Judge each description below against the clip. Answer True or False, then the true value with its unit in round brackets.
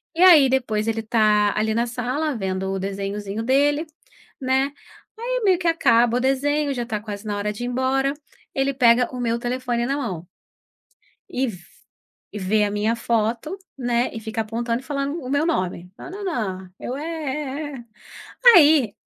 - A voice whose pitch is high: True (245 Hz)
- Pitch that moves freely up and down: False (4.5 semitones)